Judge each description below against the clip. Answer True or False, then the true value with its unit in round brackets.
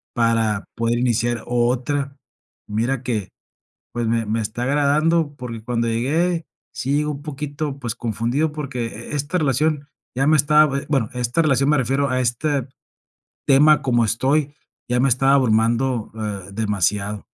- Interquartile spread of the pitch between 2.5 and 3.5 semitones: False (3.9 semitones)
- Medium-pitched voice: False (130 Hz)